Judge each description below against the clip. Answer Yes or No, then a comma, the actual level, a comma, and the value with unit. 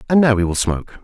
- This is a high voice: No, low, 110 Hz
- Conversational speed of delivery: No, fast, 290 wpm